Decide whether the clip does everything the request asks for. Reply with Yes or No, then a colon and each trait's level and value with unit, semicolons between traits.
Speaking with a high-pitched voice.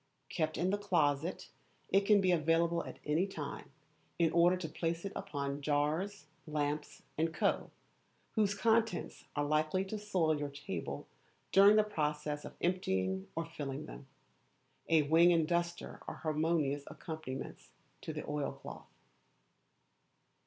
No: medium, 165 Hz